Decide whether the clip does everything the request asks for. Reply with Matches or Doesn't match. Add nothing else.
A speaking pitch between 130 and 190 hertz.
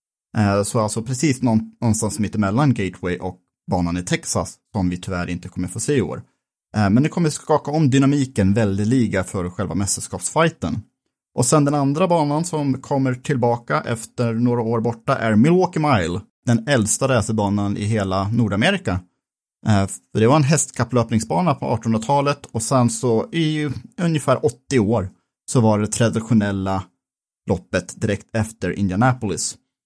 Doesn't match